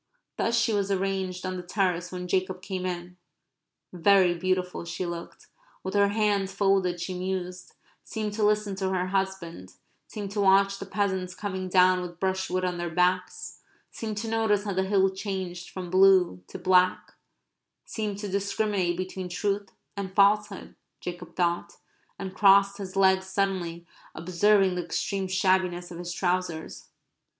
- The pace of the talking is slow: No, average, 155 wpm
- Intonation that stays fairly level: Yes, narrow, 1.7 semitones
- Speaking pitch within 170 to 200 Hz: Yes, high, 190 Hz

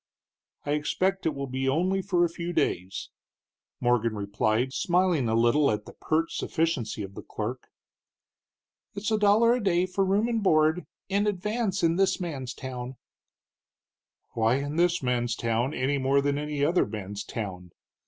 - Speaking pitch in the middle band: Yes, medium, 145 Hz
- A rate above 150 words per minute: Yes, average, 165 wpm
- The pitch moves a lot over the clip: Yes, wide, 7.1 semitones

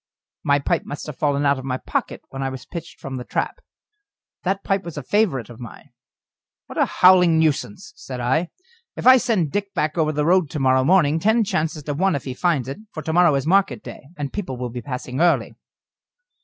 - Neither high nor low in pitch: Yes, medium, 150 Hz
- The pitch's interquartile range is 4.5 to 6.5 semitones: Yes, average, 5.1 semitones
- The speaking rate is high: Yes, fast, 220 wpm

